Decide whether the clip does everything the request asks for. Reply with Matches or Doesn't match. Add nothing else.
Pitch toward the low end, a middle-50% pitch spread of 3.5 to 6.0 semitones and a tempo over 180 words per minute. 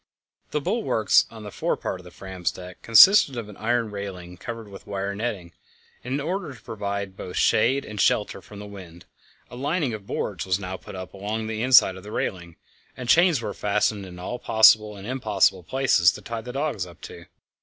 Matches